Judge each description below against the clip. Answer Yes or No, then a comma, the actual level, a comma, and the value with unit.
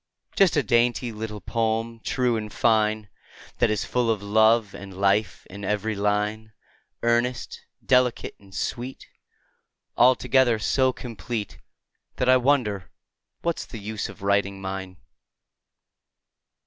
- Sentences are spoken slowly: Yes, slow, 120 wpm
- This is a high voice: No, low, 110 Hz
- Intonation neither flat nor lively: Yes, average, 3.0 semitones